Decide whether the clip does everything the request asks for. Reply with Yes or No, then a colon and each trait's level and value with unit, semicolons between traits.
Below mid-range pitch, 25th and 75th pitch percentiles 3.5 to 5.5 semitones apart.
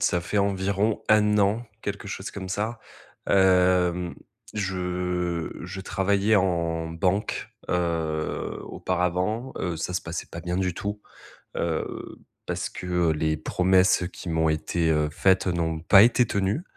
No: very low, 90 Hz; average, 2.7 semitones